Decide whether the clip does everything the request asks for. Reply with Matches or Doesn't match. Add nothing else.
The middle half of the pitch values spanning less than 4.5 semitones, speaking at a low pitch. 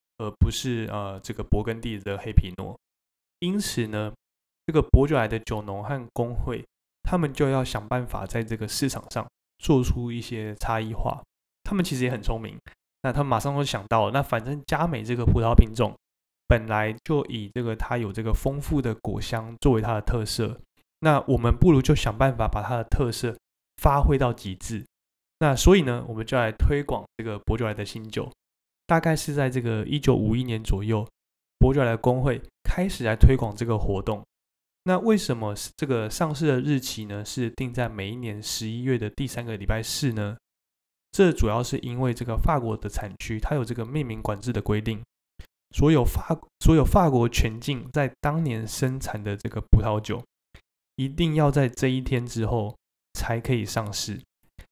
Matches